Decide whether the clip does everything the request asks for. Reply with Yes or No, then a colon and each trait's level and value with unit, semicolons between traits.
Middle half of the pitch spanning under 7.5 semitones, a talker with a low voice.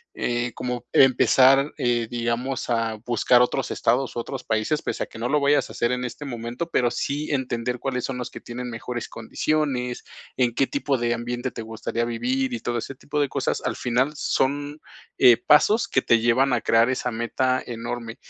Yes: narrow, 2.4 semitones; low, 125 Hz